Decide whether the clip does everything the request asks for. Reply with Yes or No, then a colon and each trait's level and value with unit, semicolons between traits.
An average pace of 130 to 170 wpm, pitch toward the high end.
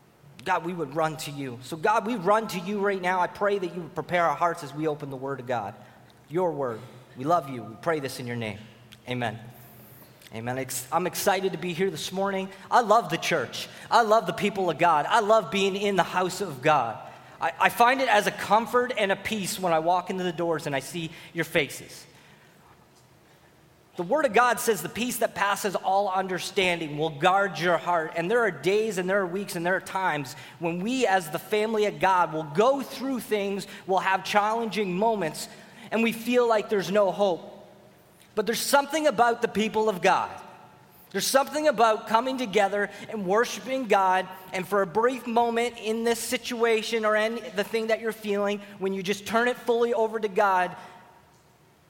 No: fast, 205 wpm; high, 195 Hz